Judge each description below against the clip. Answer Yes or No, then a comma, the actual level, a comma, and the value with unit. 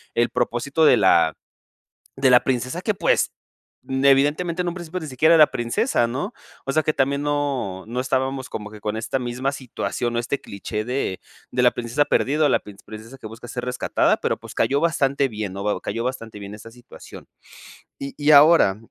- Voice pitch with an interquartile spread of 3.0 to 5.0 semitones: Yes, average, 4.1 semitones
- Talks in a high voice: No, low, 130 Hz